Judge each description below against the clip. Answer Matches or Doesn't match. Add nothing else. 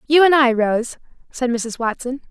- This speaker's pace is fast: Doesn't match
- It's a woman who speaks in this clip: Matches